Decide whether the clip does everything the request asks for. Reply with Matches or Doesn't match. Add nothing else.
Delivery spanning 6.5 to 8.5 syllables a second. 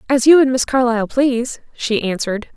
Doesn't match